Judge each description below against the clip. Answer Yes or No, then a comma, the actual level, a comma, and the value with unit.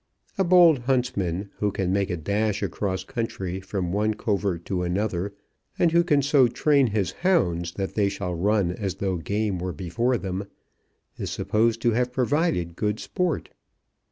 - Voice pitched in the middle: No, low, 105 Hz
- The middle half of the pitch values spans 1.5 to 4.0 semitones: No, average, 4.9 semitones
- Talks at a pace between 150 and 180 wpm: Yes, average, 165 wpm